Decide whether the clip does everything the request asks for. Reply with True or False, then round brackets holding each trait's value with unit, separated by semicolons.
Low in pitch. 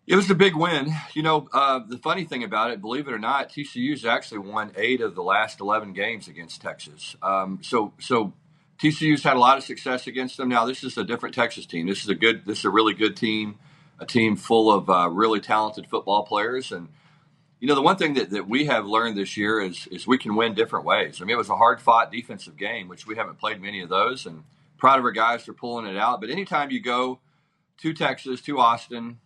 True (130 Hz)